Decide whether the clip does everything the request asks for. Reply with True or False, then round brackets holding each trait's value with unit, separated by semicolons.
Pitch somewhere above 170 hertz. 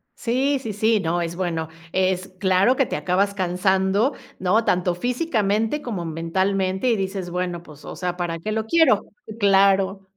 True (190 Hz)